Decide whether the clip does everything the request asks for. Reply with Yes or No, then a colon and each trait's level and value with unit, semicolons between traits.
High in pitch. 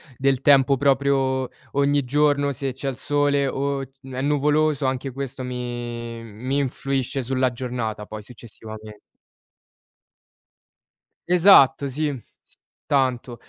No: low, 135 Hz